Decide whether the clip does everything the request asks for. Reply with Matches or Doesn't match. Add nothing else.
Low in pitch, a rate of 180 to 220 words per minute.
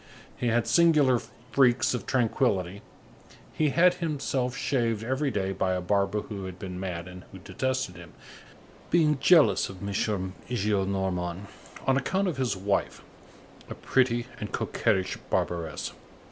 Doesn't match